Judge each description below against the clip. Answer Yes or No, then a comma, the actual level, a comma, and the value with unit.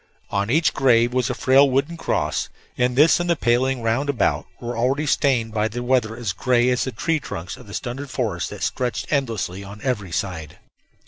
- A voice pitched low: Yes, low, 125 Hz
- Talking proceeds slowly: No, average, 200 wpm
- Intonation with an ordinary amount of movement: Yes, average, 3.6 semitones